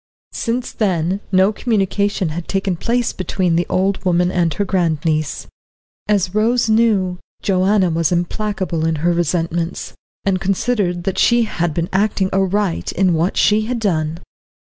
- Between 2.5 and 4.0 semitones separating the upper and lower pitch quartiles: Yes, average, 3.2 semitones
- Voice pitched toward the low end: No, medium, 185 Hz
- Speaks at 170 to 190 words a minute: No, average, 150 wpm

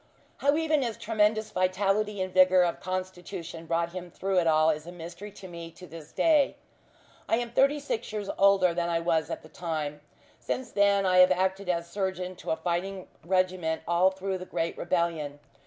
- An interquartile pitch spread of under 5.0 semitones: Yes, average, 2.8 semitones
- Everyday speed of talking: Yes, average, 190 wpm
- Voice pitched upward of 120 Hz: Yes, medium, 185 Hz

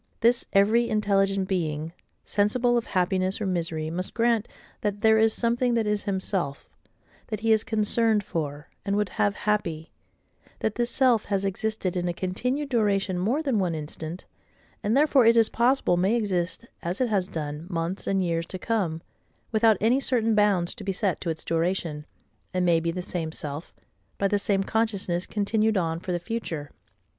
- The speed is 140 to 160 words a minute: No, average, 175 wpm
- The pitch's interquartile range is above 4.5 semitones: No, average, 4.2 semitones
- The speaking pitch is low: No, high, 200 Hz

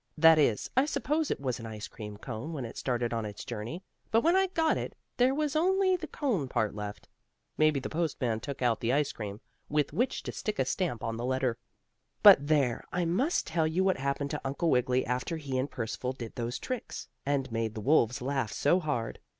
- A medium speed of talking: No, fast, 215 wpm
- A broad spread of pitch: Yes, wide, 6.9 semitones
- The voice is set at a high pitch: No, medium, 140 Hz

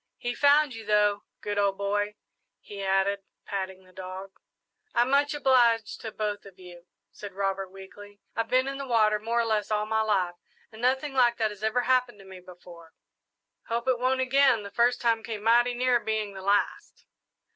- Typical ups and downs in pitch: Yes, average, 3.5 semitones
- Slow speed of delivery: No, average, 190 wpm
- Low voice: No, high, 215 Hz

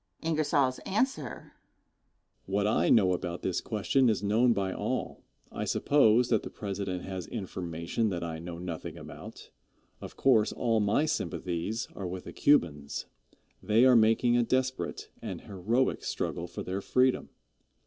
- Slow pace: No, average, 145 wpm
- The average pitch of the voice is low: Yes, low, 105 Hz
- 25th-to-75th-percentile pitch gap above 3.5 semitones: Yes, wide, 5.5 semitones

